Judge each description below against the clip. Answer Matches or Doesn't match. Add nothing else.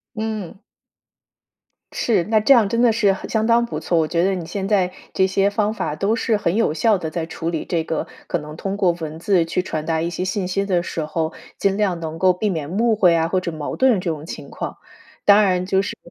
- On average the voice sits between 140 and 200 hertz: Matches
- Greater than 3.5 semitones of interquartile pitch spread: Matches